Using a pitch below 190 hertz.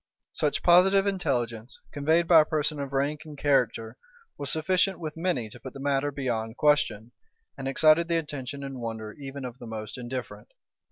Yes: medium, 140 Hz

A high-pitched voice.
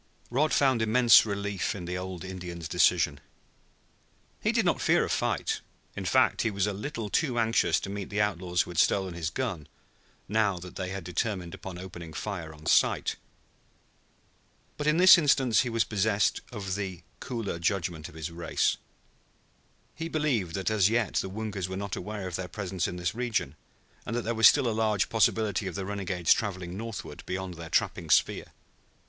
No: low, 100 Hz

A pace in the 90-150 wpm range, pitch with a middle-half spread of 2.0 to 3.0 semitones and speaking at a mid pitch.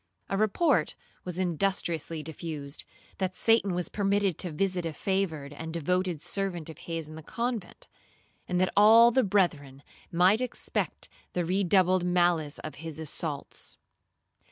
No: average, 140 wpm; average, 3.5 semitones; medium, 180 Hz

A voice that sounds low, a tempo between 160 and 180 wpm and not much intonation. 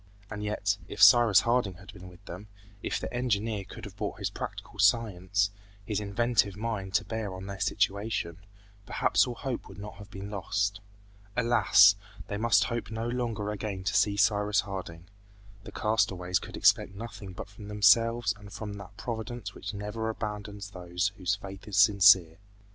Yes: low, 105 Hz; average, 170 wpm; narrow, 2.2 semitones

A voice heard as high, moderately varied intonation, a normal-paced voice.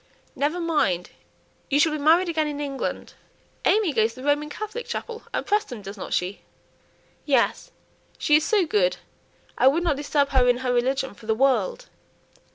Yes: very high, 290 Hz; average, 4.9 semitones; average, 165 wpm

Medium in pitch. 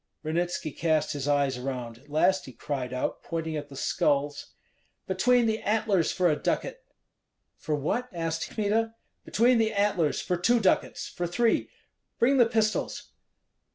Yes: medium, 175 Hz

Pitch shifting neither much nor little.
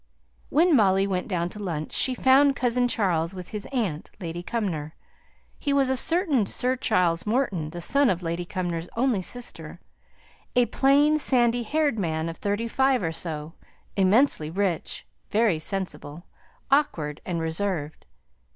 No: wide, 7.1 semitones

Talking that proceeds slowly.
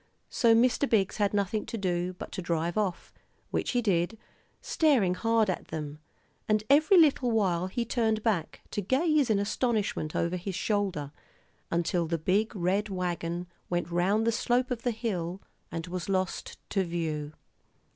No: average, 165 wpm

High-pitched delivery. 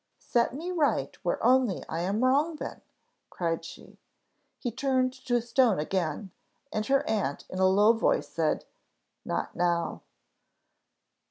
Yes: high, 225 Hz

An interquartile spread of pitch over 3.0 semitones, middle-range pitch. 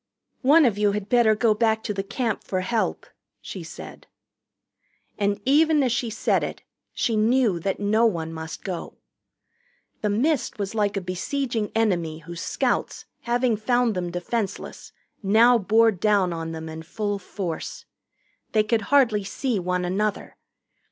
No: average, 4.0 semitones; high, 210 Hz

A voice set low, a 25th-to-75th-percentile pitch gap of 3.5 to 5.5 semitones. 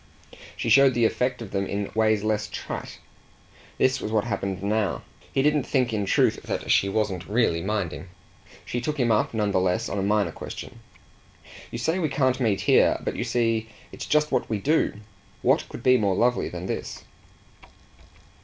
Yes: low, 110 Hz; average, 3.8 semitones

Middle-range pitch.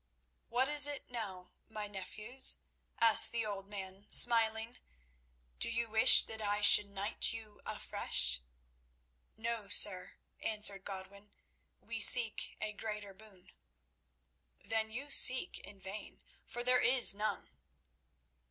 No: high, 215 Hz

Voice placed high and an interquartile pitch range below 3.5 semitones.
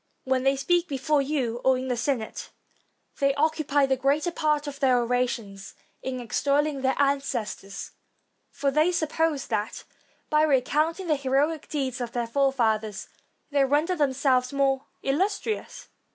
Yes: very high, 275 Hz; average, 2.9 semitones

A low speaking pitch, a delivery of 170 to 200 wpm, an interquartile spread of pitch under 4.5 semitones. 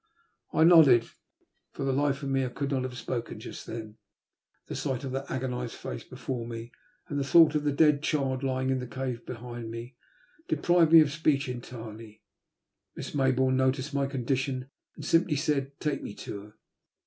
Yes: low, 130 Hz; average, 185 wpm; narrow, 2.6 semitones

